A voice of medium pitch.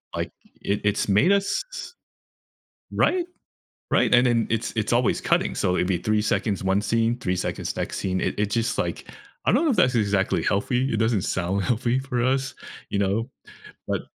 No: low, 110 Hz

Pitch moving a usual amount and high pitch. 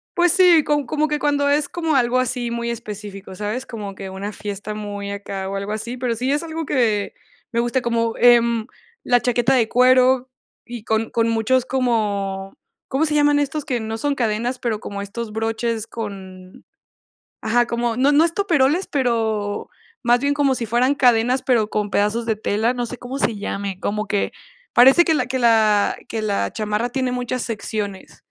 Yes: average, 3.6 semitones; high, 235 Hz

